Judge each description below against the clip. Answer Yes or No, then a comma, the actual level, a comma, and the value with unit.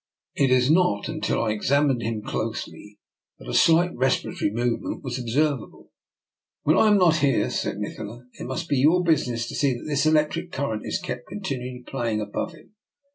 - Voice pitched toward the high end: No, low, 130 Hz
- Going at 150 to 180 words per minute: No, average, 190 wpm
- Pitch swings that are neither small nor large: Yes, average, 4.9 semitones